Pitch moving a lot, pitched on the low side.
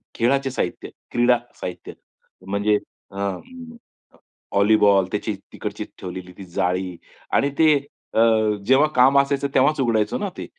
Yes: wide, 5.9 semitones; low, 110 Hz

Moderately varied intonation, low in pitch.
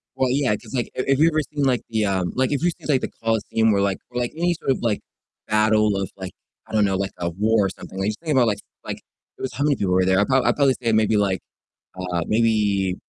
Yes: average, 4.9 semitones; low, 110 Hz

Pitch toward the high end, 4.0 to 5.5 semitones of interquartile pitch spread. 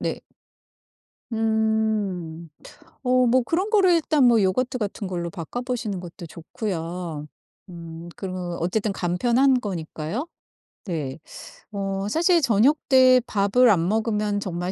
No: high, 205 Hz; wide, 6.0 semitones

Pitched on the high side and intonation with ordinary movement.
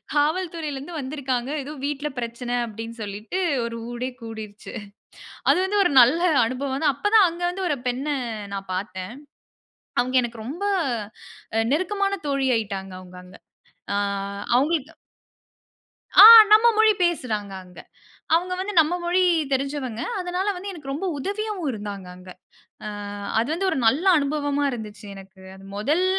No: very high, 270 Hz; wide, 7.3 semitones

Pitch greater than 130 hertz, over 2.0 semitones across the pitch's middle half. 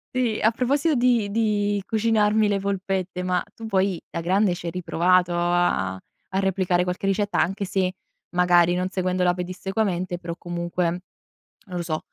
Yes: medium, 185 Hz; narrow, 2.6 semitones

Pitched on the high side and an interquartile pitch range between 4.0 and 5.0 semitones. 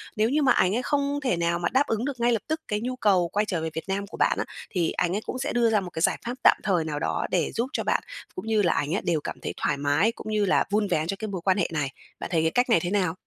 No: high, 200 Hz; wide, 5.5 semitones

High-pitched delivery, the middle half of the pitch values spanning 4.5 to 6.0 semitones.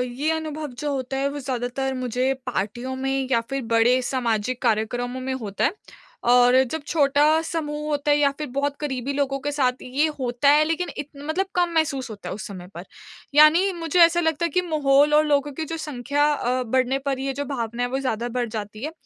No: very high, 270 Hz; average, 3.1 semitones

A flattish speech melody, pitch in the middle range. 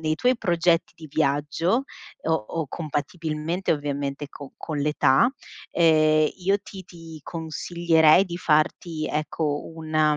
Yes: narrow, 2.2 semitones; medium, 160 Hz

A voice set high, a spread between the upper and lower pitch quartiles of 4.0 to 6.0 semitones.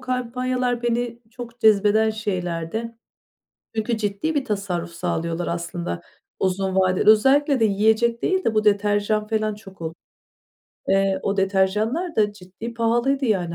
No: high, 215 Hz; average, 3.6 semitones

